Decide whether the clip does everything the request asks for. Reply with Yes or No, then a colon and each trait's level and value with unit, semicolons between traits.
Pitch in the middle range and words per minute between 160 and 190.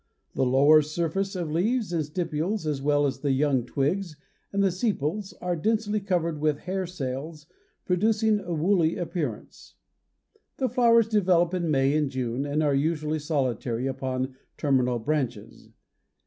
No: medium, 155 Hz; average, 150 wpm